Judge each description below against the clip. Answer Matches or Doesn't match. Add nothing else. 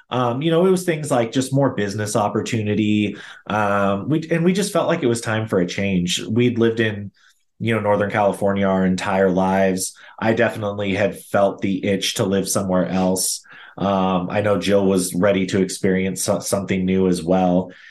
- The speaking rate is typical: Matches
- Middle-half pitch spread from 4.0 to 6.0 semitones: Doesn't match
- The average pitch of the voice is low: Matches